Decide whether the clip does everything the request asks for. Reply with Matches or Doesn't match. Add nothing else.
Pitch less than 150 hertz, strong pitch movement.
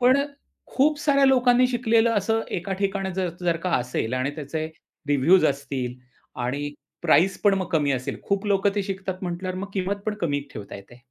Doesn't match